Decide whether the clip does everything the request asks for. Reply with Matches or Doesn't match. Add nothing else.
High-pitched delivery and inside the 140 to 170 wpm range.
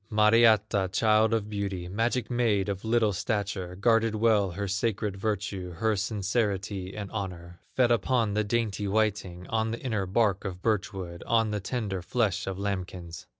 Doesn't match